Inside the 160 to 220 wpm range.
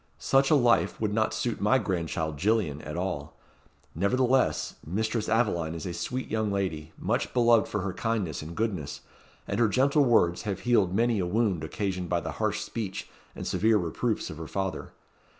Yes: average, 180 wpm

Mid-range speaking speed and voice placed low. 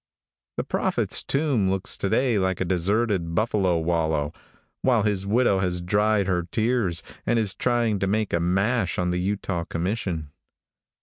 Yes: average, 160 wpm; very low, 95 Hz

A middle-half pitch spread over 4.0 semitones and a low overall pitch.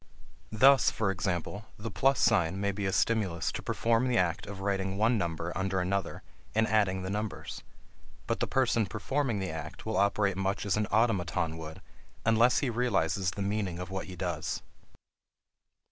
No: average, 3.2 semitones; low, 100 Hz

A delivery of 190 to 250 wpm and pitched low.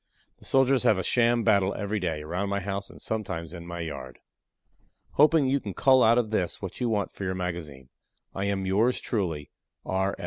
Yes: average, 200 wpm; low, 100 Hz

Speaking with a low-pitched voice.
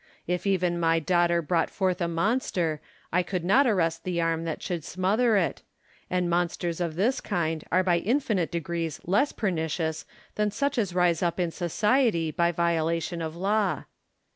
No: medium, 175 Hz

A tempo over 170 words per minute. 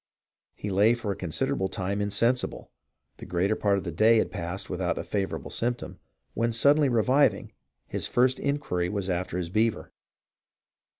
No: average, 160 wpm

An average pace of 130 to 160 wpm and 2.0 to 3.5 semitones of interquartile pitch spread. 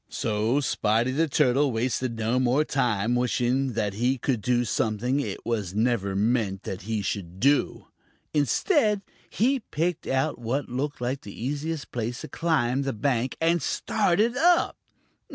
No: average, 150 wpm; average, 4.4 semitones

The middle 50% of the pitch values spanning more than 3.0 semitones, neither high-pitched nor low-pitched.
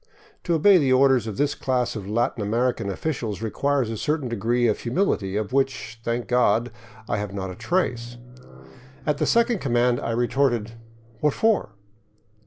No: average, 3.8 semitones; low, 120 Hz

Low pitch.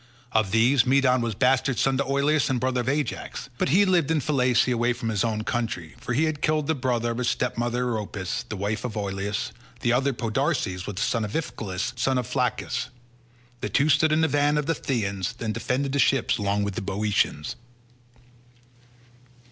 Yes: low, 125 Hz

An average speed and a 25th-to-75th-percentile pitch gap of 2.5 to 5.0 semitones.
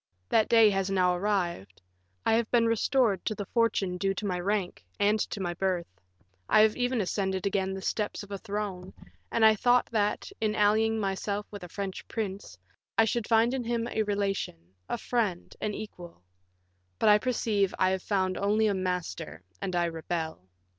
Yes: average, 185 wpm; average, 2.9 semitones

